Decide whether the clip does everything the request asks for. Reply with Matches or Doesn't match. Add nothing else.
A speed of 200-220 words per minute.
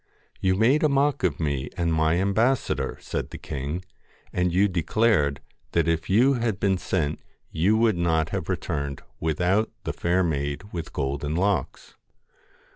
Doesn't match